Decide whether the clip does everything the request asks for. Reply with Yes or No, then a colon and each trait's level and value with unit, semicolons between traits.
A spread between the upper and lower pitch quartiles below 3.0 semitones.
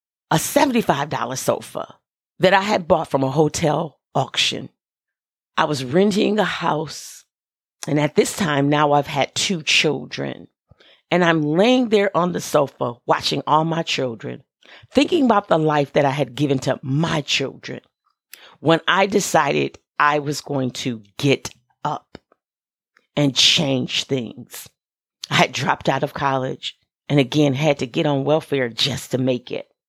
No: average, 4.0 semitones